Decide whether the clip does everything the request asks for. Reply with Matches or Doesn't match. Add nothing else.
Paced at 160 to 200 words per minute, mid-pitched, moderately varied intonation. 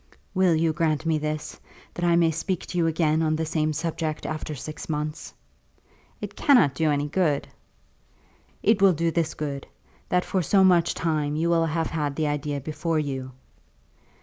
Doesn't match